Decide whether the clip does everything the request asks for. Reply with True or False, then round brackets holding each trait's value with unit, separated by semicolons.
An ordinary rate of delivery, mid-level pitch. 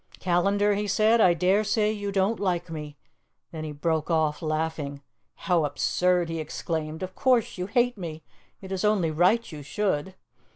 True (175 wpm; 180 Hz)